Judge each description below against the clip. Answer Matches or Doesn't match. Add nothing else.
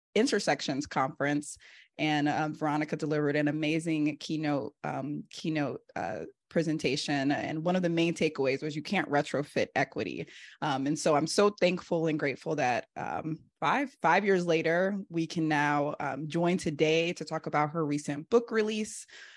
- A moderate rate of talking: Matches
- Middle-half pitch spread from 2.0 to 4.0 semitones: Matches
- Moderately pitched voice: Matches